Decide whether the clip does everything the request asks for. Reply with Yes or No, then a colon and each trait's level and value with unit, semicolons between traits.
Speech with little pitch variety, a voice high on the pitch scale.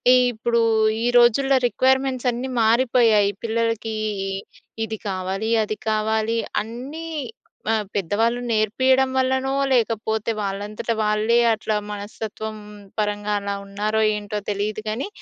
Yes: narrow, 2.2 semitones; high, 220 Hz